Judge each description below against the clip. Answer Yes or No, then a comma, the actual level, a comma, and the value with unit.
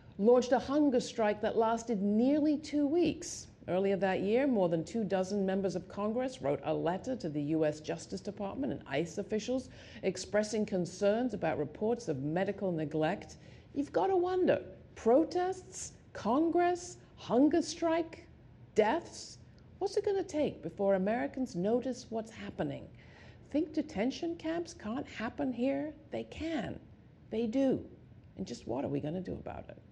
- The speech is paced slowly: No, average, 150 wpm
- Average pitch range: No, wide, 7.2 semitones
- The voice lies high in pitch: Yes, high, 230 Hz